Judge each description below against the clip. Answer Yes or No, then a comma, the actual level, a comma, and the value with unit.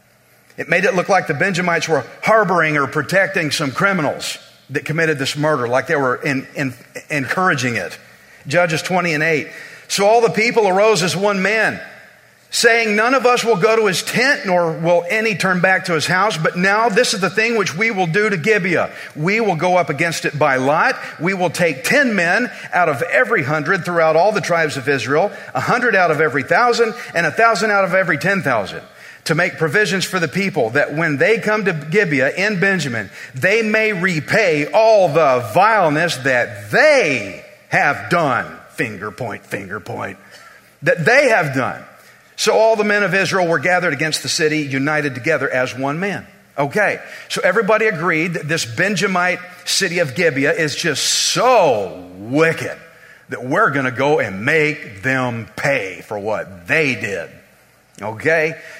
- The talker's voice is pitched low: No, medium, 175 Hz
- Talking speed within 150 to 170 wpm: No, average, 180 wpm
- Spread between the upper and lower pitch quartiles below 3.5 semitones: No, average, 4.8 semitones